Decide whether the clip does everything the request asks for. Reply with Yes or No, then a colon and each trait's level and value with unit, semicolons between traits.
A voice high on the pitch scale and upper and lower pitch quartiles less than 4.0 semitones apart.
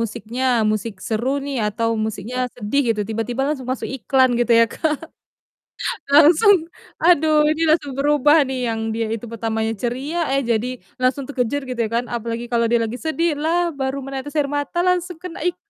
No: very high, 260 Hz; average, 4.6 semitones